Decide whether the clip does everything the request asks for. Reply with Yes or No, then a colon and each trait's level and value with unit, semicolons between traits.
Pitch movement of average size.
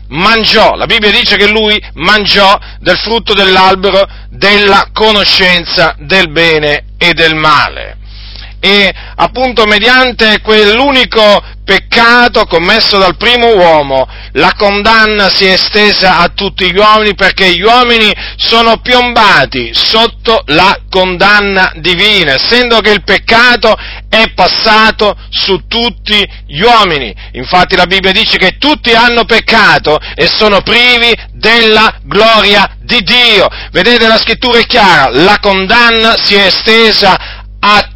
Yes: average, 3.5 semitones